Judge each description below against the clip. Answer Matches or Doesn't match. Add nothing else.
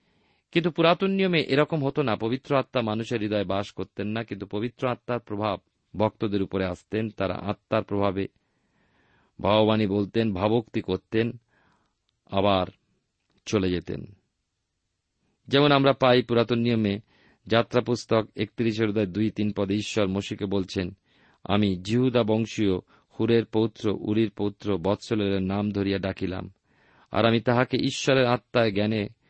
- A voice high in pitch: Doesn't match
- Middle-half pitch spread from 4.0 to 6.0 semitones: Doesn't match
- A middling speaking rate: Doesn't match